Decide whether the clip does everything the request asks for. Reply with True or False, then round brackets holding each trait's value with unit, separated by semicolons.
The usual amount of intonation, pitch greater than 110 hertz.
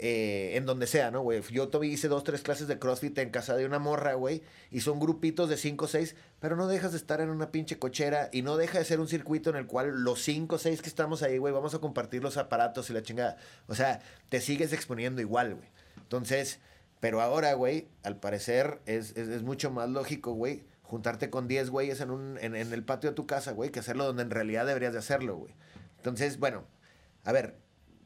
True (4.0 semitones; 135 Hz)